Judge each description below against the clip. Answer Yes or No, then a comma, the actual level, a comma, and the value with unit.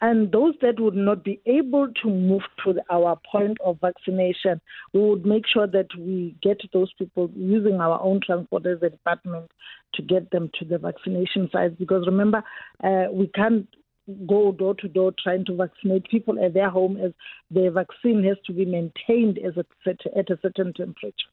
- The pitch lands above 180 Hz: Yes, high, 190 Hz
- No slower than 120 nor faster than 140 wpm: No, average, 175 wpm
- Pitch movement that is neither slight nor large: No, narrow, 2.1 semitones